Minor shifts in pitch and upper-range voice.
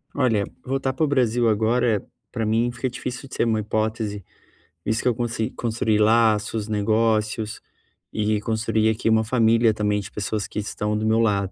No: narrow, 1.6 semitones; low, 110 Hz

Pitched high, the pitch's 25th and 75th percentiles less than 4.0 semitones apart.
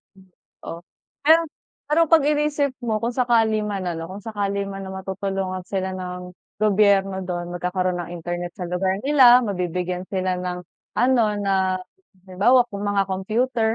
Yes: high, 195 Hz; average, 3.6 semitones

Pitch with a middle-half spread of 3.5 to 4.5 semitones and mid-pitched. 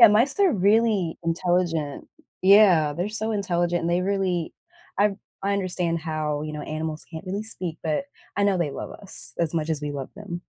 Yes: average, 3.9 semitones; medium, 175 Hz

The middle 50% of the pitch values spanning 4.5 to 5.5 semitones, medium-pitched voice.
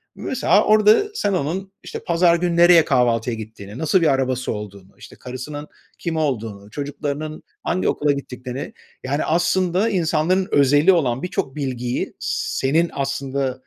Yes: average, 5.1 semitones; medium, 145 Hz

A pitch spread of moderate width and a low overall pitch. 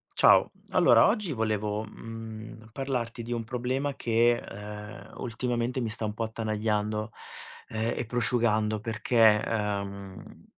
No: narrow, 1.9 semitones; low, 110 Hz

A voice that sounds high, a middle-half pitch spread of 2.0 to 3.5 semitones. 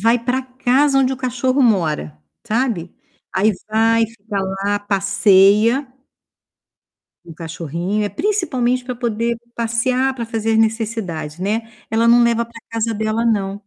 Yes: high, 225 Hz; average, 3.2 semitones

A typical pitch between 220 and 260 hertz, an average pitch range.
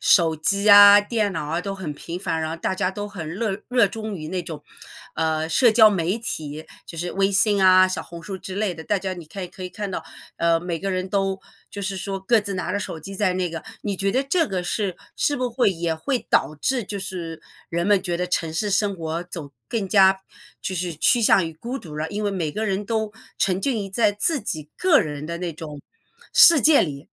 No: high, 190 Hz; average, 3.6 semitones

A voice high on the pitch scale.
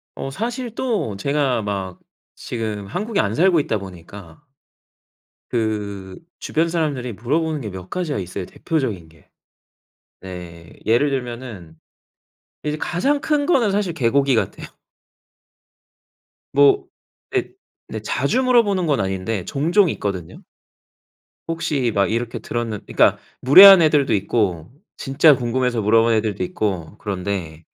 No: low, 120 Hz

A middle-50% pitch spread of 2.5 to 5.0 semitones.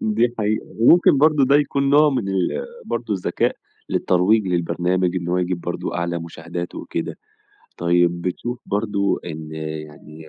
No: wide, 5.6 semitones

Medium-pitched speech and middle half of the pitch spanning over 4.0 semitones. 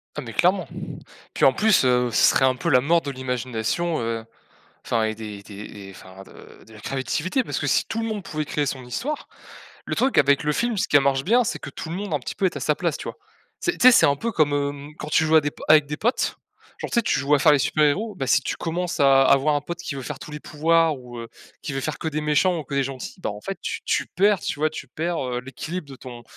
Yes: medium, 145 Hz; average, 4.6 semitones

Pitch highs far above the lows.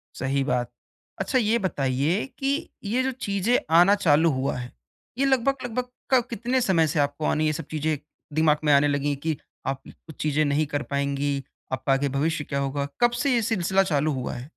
Yes: wide, 6.9 semitones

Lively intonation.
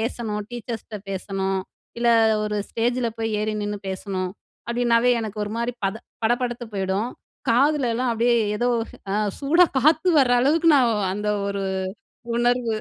No: average, 2.8 semitones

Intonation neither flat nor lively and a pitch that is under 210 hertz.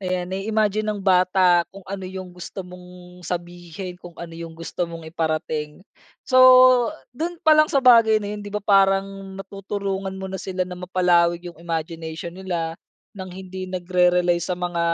No: narrow, 2.2 semitones; medium, 185 Hz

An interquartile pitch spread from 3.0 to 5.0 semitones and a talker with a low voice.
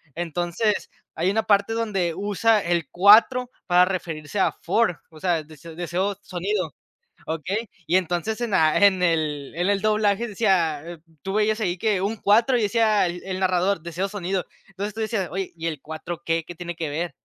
No: average, 3.6 semitones; medium, 185 Hz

